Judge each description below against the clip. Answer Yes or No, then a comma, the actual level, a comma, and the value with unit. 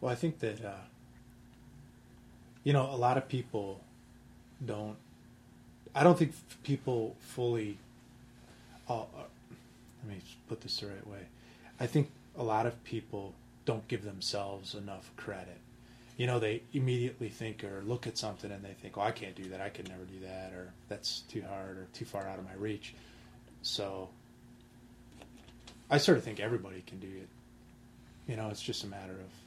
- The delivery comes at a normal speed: Yes, average, 175 wpm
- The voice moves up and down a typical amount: Yes, average, 3.7 semitones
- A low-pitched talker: Yes, low, 110 Hz